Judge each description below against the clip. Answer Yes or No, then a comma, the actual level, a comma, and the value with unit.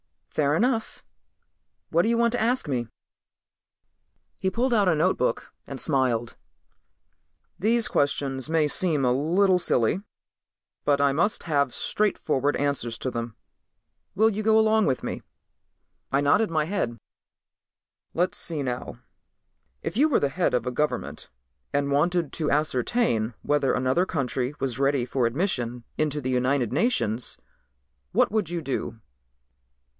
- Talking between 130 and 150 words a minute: Yes, average, 140 wpm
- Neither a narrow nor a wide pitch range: No, wide, 6.5 semitones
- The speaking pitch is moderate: Yes, medium, 145 Hz